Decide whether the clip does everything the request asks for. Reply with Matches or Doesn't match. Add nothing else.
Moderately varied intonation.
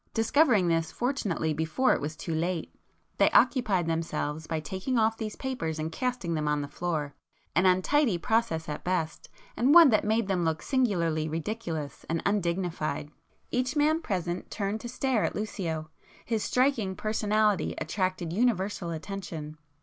Doesn't match